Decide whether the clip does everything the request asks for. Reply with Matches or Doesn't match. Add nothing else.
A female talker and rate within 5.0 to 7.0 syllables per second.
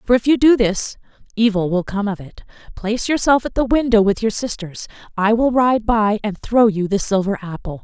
Matches